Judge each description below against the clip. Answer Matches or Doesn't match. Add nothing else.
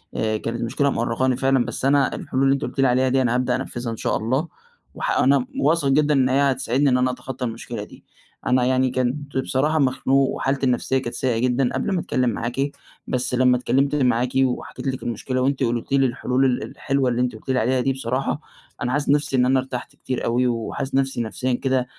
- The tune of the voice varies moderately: Doesn't match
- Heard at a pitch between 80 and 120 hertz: Doesn't match